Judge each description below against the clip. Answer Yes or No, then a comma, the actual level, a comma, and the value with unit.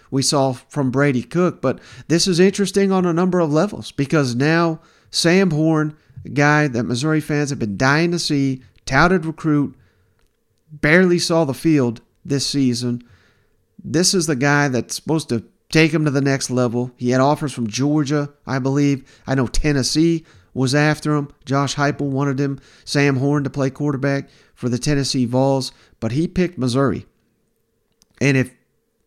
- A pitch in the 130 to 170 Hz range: Yes, medium, 140 Hz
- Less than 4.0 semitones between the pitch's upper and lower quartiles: Yes, average, 3.5 semitones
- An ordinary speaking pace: Yes, average, 165 wpm